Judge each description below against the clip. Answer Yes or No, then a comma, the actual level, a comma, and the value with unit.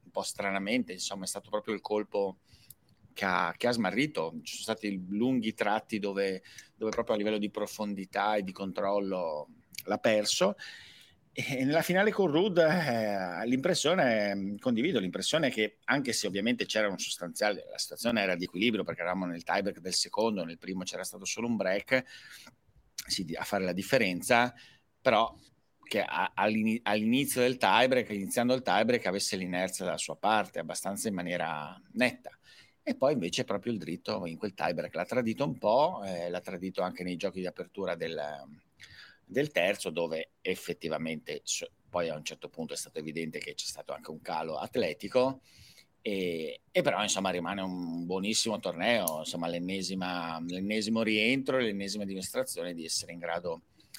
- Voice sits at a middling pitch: No, low, 100 Hz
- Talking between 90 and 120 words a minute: No, average, 160 wpm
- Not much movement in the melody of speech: No, average, 3.6 semitones